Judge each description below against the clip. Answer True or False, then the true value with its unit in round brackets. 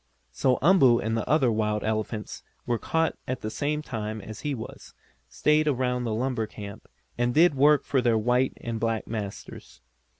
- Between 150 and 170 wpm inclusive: False (180 wpm)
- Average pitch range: True (3.9 semitones)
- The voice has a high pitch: False (120 Hz)